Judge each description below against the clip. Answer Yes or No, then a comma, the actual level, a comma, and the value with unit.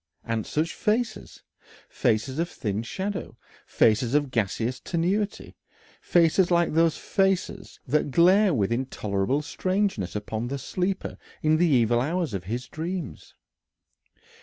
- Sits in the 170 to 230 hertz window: No, medium, 150 Hz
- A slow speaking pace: Yes, slow, 125 wpm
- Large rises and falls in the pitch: Yes, wide, 7.4 semitones